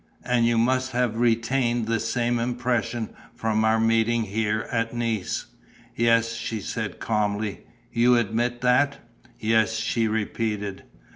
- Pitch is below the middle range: Yes, low, 115 Hz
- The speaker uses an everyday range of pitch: No, narrow, 1.4 semitones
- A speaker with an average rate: No, slow, 130 wpm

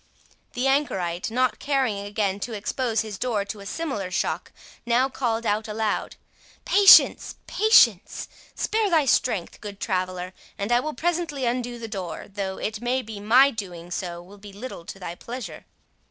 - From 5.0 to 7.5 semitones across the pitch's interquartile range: No, average, 4.6 semitones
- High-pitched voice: Yes, high, 220 Hz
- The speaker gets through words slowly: No, average, 160 wpm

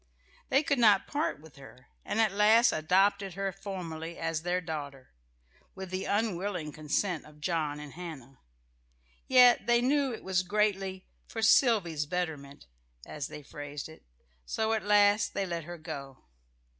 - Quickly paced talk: No, average, 155 wpm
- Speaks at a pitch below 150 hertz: No, medium, 180 Hz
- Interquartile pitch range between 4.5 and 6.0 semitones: Yes, average, 5.2 semitones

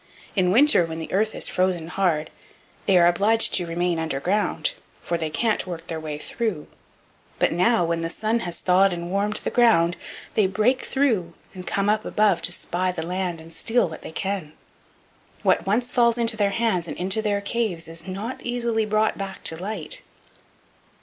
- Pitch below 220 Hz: Yes, high, 190 Hz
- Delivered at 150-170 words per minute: No, average, 185 wpm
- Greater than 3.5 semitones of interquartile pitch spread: Yes, average, 4.4 semitones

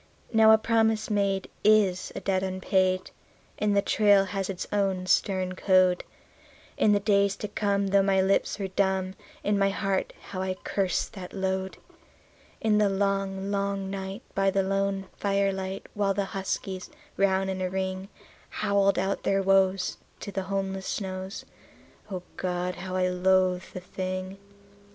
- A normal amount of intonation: No, narrow, 1.0 semitones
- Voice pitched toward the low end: No, high, 195 Hz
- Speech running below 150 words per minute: No, average, 155 wpm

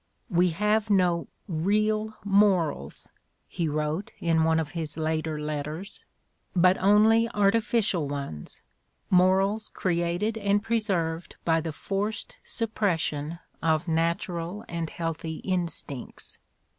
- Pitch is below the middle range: No, medium, 175 Hz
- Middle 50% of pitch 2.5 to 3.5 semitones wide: No, average, 4.2 semitones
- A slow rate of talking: Yes, slow, 105 wpm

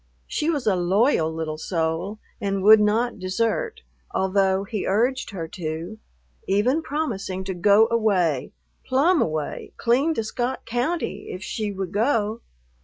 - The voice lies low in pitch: No, high, 205 Hz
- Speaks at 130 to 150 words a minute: Yes, average, 140 wpm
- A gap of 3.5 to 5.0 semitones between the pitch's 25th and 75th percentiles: Yes, average, 4.5 semitones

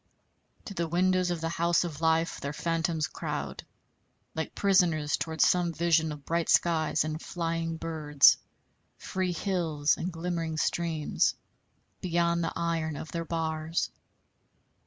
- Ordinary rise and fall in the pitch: No, narrow, 1.4 semitones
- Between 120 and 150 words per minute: Yes, slow, 135 wpm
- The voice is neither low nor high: Yes, medium, 165 Hz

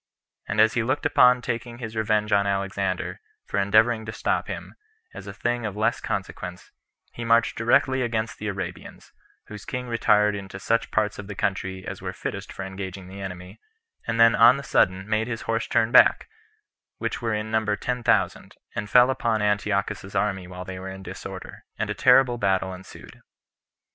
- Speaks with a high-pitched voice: No, low, 105 Hz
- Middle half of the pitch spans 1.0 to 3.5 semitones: Yes, average, 3.0 semitones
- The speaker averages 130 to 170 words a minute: No, average, 185 wpm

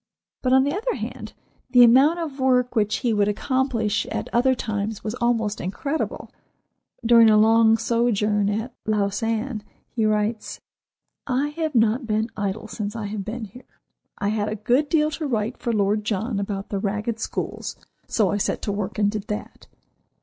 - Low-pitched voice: No, high, 220 Hz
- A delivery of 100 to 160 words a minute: No, average, 175 wpm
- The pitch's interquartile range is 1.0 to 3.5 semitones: Yes, average, 3.1 semitones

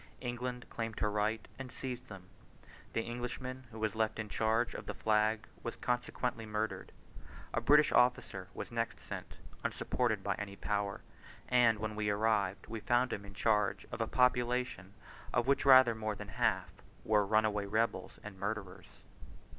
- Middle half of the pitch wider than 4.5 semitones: No, average, 2.7 semitones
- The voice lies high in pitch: No, low, 110 Hz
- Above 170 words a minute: No, average, 160 wpm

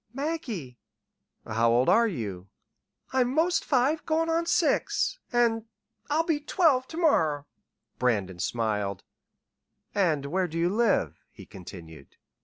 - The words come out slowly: Yes, slow, 125 wpm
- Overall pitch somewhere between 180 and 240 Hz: Yes, high, 190 Hz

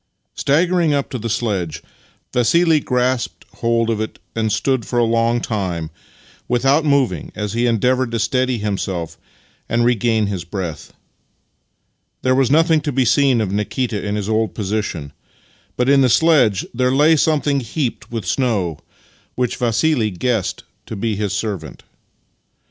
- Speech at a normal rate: Yes, average, 155 wpm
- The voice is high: No, low, 115 Hz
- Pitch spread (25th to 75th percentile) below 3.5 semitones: No, average, 3.8 semitones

